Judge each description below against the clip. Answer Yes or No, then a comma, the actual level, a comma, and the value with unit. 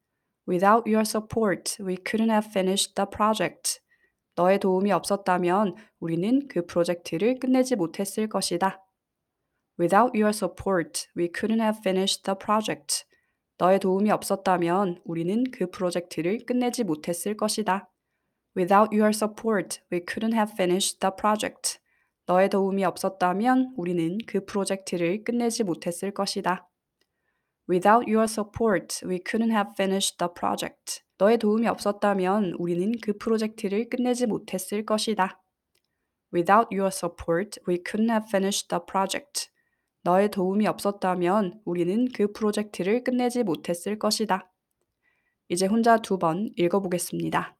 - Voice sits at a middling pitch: No, high, 195 Hz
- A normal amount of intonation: Yes, average, 3.0 semitones